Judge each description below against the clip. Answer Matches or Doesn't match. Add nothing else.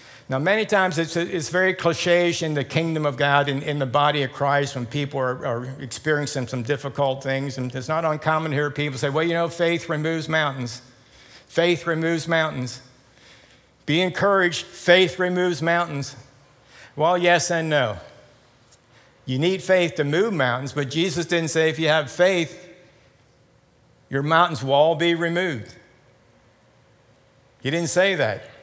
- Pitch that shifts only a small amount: Doesn't match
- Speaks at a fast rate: Doesn't match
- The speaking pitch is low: Doesn't match